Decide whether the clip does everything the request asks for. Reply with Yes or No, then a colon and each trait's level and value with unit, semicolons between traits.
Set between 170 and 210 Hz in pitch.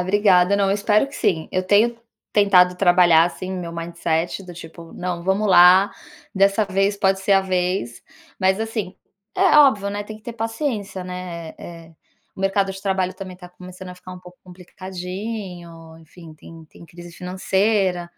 Yes: medium, 185 Hz